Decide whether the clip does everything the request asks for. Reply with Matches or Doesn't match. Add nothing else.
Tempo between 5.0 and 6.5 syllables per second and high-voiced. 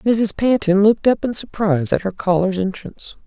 Matches